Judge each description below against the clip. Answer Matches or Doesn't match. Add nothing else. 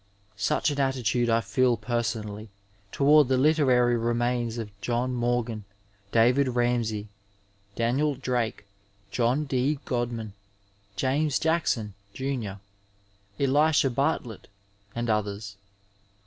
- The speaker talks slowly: Matches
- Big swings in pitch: Doesn't match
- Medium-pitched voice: Doesn't match